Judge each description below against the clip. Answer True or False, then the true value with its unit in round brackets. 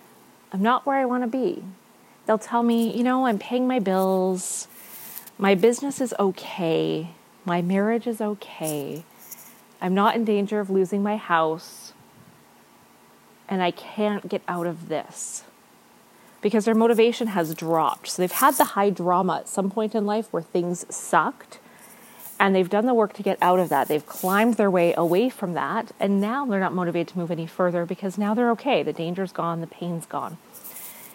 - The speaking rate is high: False (180 wpm)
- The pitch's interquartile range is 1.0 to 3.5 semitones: False (4.5 semitones)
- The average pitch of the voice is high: True (200 Hz)